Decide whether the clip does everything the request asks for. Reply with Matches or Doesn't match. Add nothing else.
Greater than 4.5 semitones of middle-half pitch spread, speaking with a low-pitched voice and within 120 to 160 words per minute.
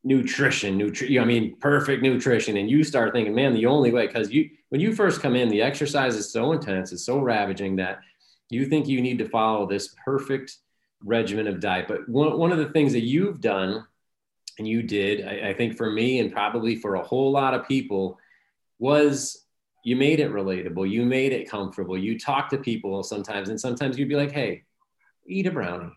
Doesn't match